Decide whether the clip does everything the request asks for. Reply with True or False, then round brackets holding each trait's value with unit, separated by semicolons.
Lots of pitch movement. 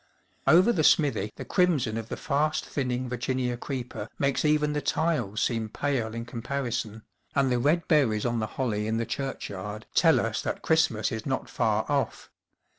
False (4.4 semitones)